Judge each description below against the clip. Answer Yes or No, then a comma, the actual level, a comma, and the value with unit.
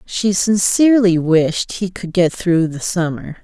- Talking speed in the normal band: Yes, average, 155 wpm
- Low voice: No, medium, 185 Hz